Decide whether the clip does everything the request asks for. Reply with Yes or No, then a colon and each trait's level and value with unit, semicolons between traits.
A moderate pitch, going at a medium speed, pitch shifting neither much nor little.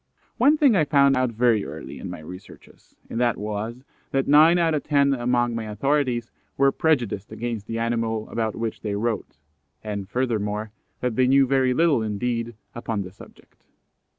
No: low, 120 Hz; average, 175 wpm; average, 4.0 semitones